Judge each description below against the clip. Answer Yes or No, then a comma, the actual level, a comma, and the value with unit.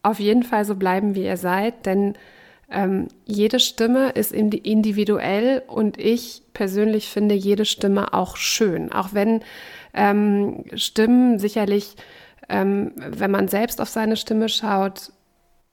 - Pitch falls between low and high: No, high, 210 Hz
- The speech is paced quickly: No, average, 135 wpm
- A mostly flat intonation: Yes, narrow, 2.1 semitones